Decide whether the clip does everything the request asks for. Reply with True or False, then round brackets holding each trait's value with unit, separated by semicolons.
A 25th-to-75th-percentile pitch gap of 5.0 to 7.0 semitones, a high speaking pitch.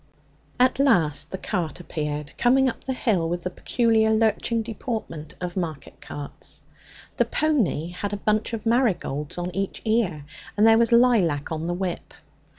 True (5.6 semitones; 195 Hz)